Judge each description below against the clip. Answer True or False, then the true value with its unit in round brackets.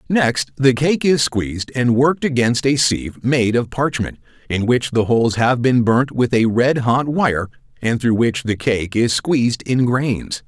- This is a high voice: False (125 Hz)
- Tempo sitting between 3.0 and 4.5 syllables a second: True (4.3 syllables/s)